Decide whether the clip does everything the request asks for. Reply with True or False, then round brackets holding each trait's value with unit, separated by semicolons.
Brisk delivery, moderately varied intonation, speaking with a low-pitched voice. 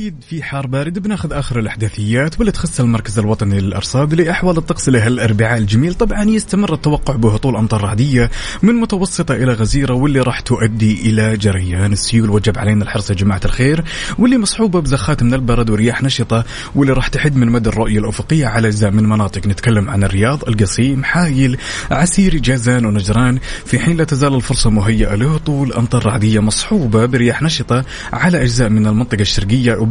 True (165 wpm; 4.8 semitones; 120 Hz)